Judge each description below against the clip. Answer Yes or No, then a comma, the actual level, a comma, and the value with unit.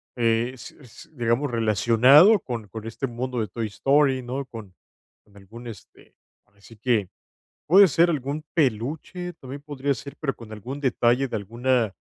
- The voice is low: Yes, low, 125 Hz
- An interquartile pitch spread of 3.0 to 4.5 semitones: Yes, average, 3.7 semitones